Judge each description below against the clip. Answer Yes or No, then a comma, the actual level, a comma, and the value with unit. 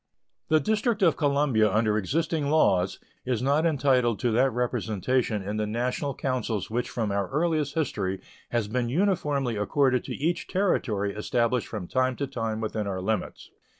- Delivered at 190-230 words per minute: No, average, 160 wpm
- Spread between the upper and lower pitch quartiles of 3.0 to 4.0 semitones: No, average, 5.0 semitones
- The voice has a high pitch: No, low, 125 Hz